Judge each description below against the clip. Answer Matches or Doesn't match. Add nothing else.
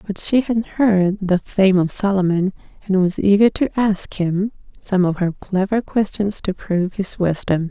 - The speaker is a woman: Matches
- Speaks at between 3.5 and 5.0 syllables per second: Matches